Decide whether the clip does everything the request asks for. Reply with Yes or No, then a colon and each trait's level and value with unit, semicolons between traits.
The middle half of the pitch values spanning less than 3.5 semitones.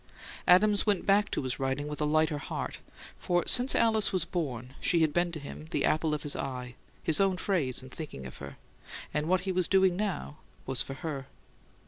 No: average, 5.0 semitones